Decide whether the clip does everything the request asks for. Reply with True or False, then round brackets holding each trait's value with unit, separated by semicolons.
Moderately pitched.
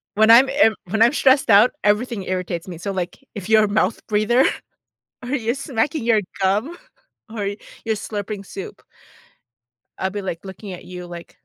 False (215 Hz)